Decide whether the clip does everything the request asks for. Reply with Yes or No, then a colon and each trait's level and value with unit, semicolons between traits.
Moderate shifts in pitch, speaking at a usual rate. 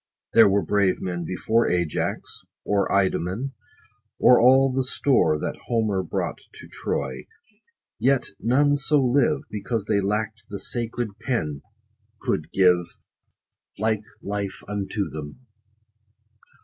No: average, 4.6 semitones; slow, 120 wpm